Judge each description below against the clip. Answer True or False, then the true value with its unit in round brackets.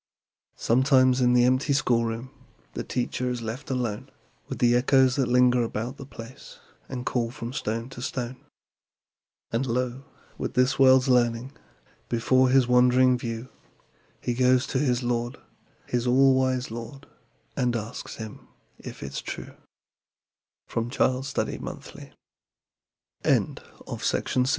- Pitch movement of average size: False (1.6 semitones)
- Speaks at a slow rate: True (115 wpm)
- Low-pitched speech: True (125 Hz)